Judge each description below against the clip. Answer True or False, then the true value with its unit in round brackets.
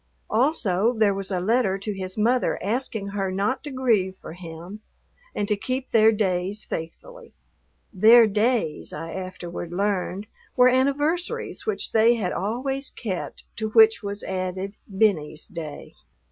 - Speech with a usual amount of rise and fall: True (4.4 semitones)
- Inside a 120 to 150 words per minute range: True (145 wpm)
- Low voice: False (210 Hz)